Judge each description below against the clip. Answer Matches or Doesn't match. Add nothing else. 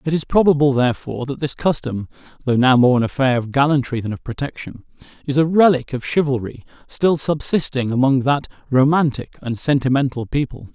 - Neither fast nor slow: Matches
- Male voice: Matches